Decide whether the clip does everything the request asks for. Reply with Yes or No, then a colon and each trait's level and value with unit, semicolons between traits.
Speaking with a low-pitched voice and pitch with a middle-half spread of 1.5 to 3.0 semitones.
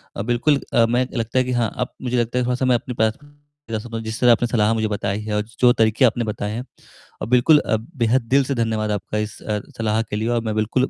Yes: low, 115 Hz; narrow, 2.4 semitones